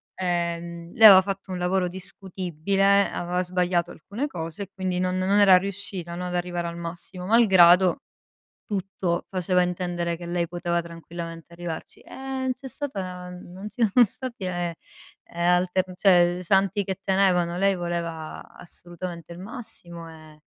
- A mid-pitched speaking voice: Yes, medium, 180 Hz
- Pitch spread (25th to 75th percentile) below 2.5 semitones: Yes, narrow, 2.1 semitones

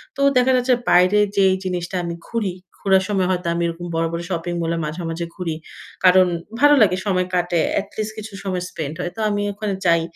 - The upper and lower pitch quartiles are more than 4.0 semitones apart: No, average, 2.9 semitones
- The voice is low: No, medium, 185 Hz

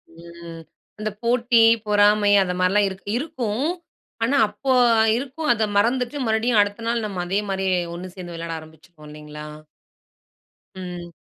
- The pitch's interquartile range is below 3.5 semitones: No, average, 5.1 semitones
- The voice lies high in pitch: Yes, high, 205 Hz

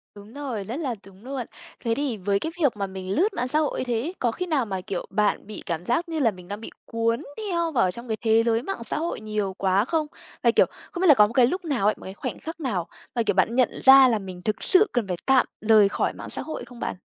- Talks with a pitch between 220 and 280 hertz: Yes, high, 230 Hz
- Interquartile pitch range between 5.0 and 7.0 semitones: Yes, wide, 5.6 semitones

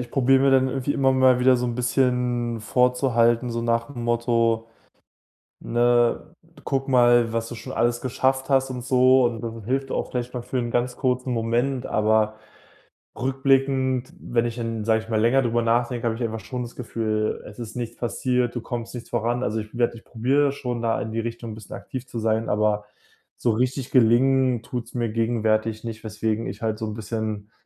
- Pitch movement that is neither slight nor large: No, narrow, 1.9 semitones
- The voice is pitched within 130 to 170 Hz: No, low, 120 Hz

